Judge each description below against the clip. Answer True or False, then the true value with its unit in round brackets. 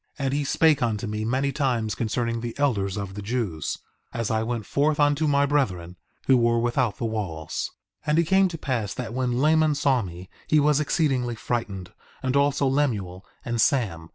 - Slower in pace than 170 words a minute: False (195 wpm)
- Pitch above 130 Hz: False (120 Hz)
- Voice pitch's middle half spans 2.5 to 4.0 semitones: False (5.0 semitones)